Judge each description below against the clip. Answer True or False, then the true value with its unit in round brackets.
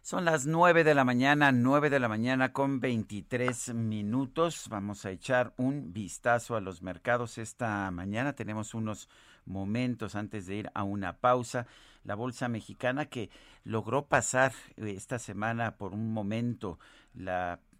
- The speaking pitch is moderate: False (115 Hz)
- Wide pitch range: False (3.8 semitones)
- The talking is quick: False (150 wpm)